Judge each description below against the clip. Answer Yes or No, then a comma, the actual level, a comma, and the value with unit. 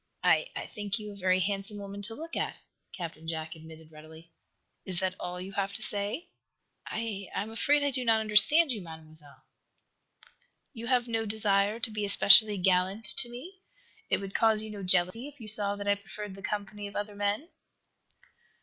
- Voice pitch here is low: No, high, 205 Hz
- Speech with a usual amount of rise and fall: Yes, average, 3.0 semitones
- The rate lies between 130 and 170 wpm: No, average, 190 wpm